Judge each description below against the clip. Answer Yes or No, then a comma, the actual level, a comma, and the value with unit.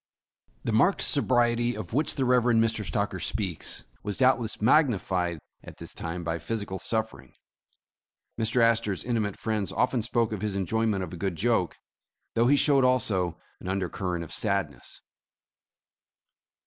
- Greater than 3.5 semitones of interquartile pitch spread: Yes, average, 4.0 semitones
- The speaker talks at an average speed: Yes, average, 150 wpm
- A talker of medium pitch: No, low, 110 Hz